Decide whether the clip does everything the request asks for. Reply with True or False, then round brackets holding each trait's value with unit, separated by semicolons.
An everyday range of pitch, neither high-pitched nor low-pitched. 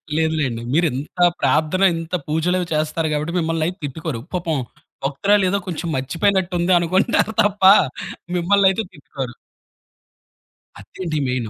True (3.5 semitones; 165 Hz)